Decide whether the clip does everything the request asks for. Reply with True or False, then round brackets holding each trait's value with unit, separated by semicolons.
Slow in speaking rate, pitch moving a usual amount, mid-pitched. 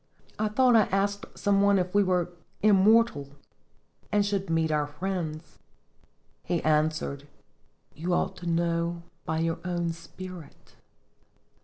True (130 wpm; 3.6 semitones; 175 Hz)